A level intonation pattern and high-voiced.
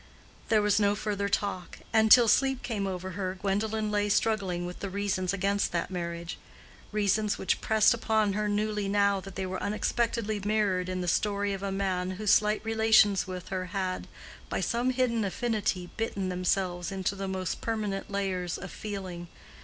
Yes: narrow, 2.3 semitones; high, 200 Hz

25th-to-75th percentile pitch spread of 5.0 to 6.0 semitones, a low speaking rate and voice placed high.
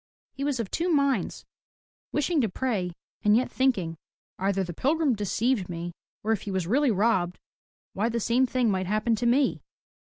No: wide, 5.5 semitones; average, 180 wpm; high, 225 Hz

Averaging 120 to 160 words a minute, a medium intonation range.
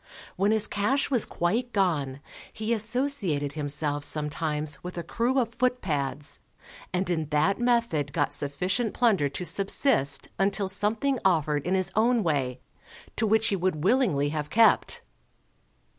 No: average, 145 wpm; wide, 7.1 semitones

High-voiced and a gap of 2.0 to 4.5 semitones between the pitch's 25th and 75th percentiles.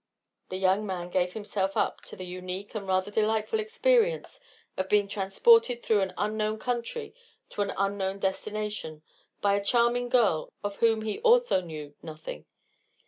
Yes: high, 205 Hz; average, 3.8 semitones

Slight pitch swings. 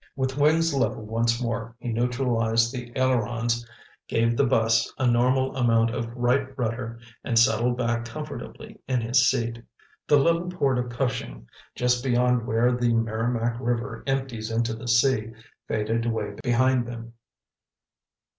Yes: narrow, 2.1 semitones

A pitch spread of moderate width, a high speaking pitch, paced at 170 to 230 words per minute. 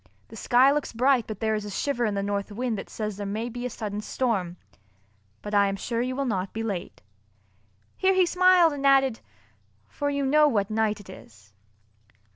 Yes: average, 4.9 semitones; high, 225 Hz; fast, 205 wpm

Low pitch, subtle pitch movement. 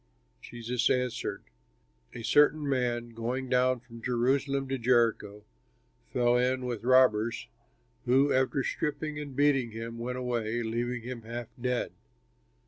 Yes: low, 125 Hz; narrow, 1.8 semitones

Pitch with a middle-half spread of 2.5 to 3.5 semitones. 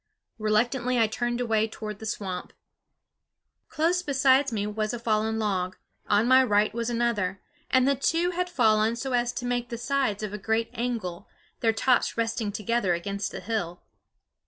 Yes: average, 2.8 semitones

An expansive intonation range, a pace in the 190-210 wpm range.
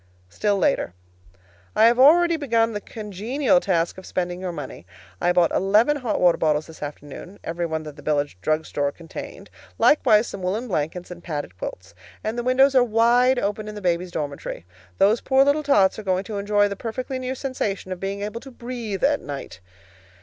Yes: wide, 6.1 semitones; average, 195 wpm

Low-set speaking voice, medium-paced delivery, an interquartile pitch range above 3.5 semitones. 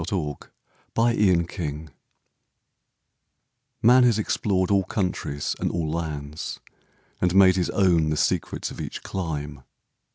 No: very low, 90 Hz; slow, 120 wpm; average, 4.1 semitones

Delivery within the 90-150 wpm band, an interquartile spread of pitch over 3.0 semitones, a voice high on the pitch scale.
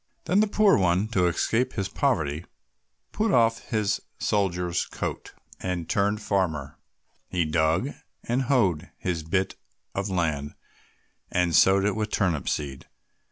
No: average, 140 wpm; average, 4.6 semitones; very low, 95 Hz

